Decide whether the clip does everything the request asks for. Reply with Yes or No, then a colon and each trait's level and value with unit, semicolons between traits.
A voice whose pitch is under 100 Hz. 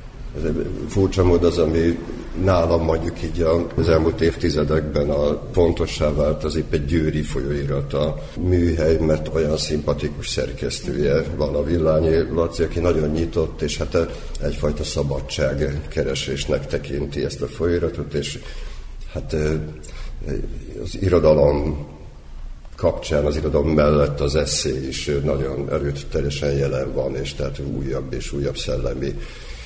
Yes: very low, 75 Hz